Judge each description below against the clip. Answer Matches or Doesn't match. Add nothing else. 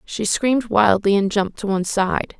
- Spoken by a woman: Matches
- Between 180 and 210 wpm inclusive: Matches